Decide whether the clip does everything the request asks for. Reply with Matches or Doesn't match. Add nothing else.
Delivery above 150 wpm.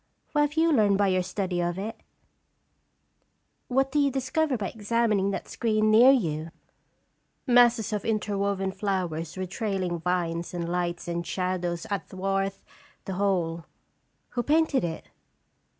Doesn't match